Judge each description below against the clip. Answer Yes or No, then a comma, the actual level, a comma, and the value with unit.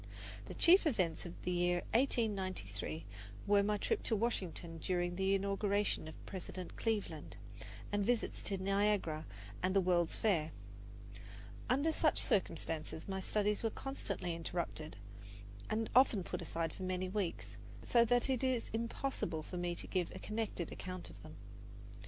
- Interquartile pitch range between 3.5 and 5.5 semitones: Yes, average, 4.0 semitones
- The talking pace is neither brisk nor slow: Yes, average, 150 wpm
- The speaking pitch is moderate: No, high, 195 Hz